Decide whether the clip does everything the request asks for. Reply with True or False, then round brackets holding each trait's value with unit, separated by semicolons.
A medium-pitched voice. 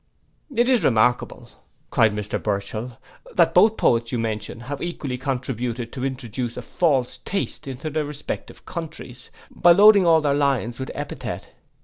False (130 Hz)